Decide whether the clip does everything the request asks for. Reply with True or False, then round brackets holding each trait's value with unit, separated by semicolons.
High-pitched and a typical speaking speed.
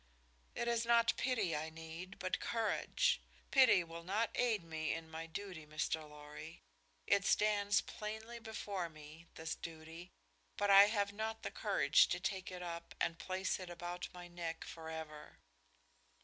False (175 Hz; 155 wpm)